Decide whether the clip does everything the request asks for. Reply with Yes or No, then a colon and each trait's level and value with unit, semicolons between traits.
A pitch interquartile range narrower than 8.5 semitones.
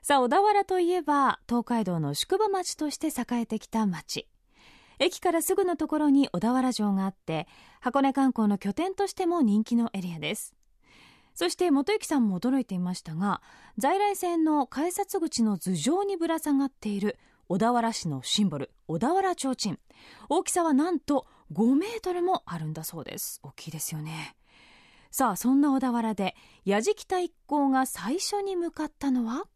No: wide, 8.9 semitones